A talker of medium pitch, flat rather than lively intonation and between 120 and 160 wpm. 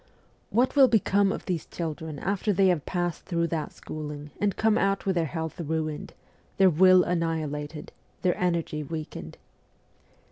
No: medium, 170 Hz; average, 3.7 semitones; average, 150 wpm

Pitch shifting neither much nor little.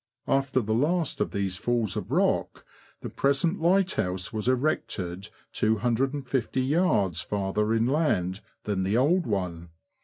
No: wide, 6.1 semitones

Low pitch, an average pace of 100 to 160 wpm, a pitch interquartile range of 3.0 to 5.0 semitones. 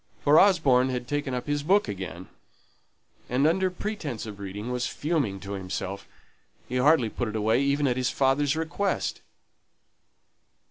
No: low, 130 Hz; average, 150 wpm; wide, 5.5 semitones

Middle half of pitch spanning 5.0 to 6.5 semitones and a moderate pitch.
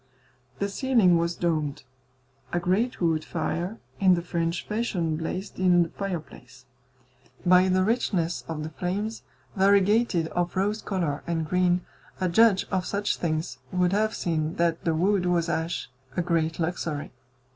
No: average, 2.9 semitones; medium, 175 Hz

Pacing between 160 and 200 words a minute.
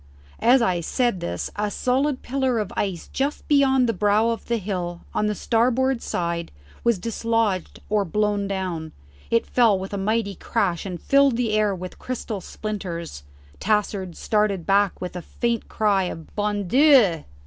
Yes: average, 165 wpm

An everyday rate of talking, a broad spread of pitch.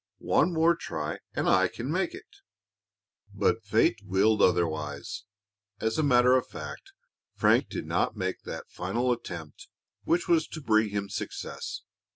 Yes: average, 150 wpm; wide, 7.7 semitones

